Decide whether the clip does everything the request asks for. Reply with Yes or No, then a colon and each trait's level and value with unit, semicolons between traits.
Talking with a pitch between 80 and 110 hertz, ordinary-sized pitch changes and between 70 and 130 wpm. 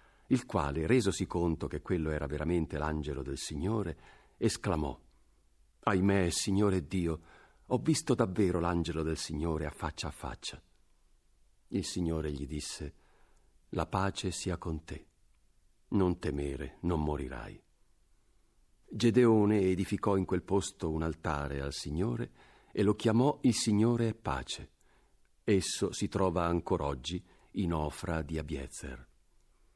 Yes: very low, 85 Hz; average, 4.6 semitones; average, 125 wpm